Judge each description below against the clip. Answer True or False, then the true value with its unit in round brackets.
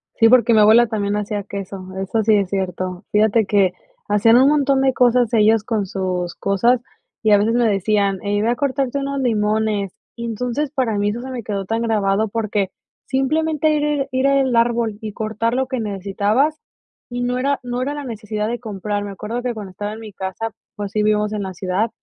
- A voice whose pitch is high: True (220 Hz)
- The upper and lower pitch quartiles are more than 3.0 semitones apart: True (3.4 semitones)